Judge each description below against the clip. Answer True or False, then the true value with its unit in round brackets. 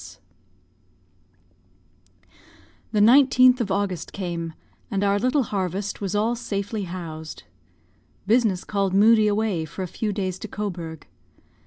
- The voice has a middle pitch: False (200 Hz)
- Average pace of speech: False (125 wpm)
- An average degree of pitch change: True (3.0 semitones)